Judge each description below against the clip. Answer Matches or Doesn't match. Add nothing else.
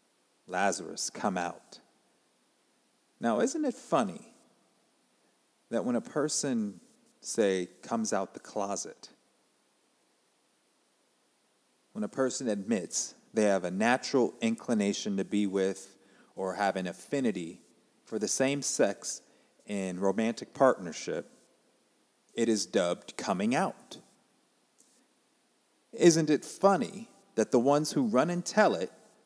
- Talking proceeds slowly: Matches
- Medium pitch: Doesn't match